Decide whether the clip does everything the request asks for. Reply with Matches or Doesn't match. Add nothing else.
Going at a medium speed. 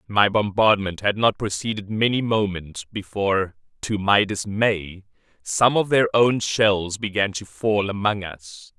Matches